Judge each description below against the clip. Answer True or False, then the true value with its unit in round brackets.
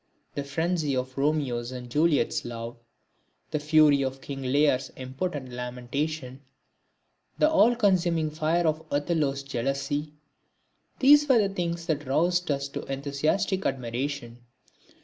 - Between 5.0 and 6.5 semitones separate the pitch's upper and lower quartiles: False (4.0 semitones)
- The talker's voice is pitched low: False (145 Hz)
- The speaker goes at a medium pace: False (125 wpm)